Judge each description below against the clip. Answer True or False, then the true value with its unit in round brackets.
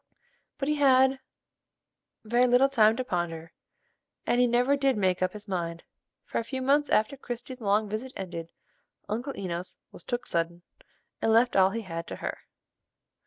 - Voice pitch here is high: True (225 Hz)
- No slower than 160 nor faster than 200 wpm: True (165 wpm)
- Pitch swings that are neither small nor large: False (5.8 semitones)